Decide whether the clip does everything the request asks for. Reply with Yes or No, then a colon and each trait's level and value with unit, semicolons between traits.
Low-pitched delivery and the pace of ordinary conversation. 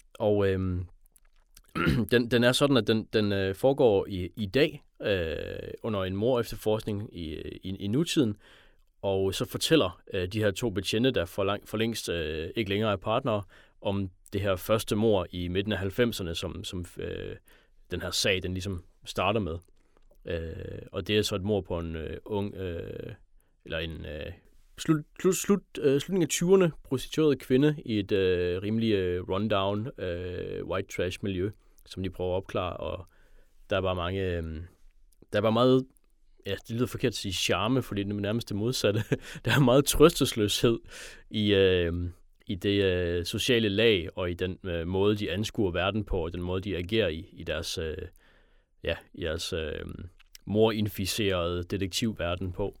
Yes: low, 100 Hz; average, 175 wpm